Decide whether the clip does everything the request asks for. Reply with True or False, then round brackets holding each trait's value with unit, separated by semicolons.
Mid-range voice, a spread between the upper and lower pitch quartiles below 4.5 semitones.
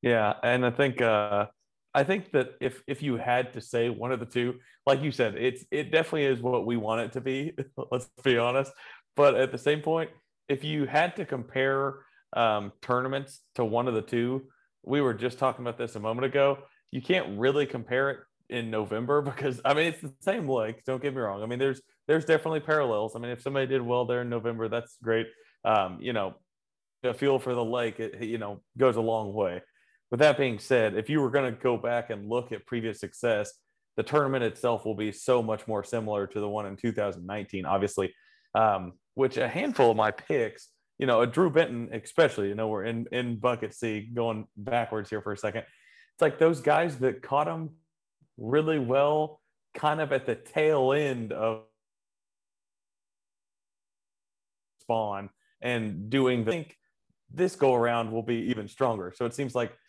False (125 Hz; 3.8 semitones)